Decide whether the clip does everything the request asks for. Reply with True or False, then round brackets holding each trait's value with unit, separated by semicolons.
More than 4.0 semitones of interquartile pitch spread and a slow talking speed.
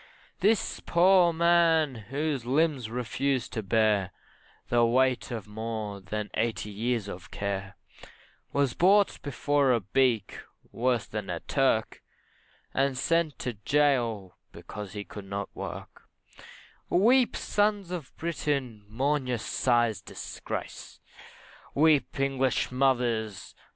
True (5.3 semitones; 120 wpm)